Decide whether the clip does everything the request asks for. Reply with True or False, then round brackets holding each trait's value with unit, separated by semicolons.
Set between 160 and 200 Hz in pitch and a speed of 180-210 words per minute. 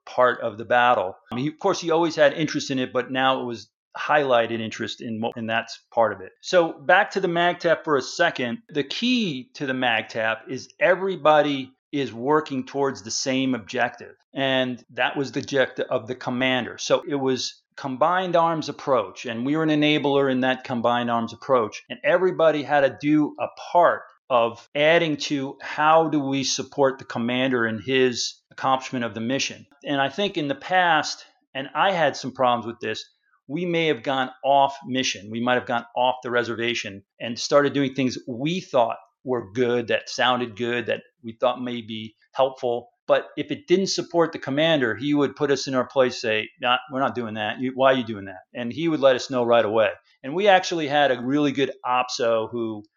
False (130 Hz; 200 wpm)